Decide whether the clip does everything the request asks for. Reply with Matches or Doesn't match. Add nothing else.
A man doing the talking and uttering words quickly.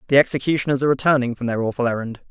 Matches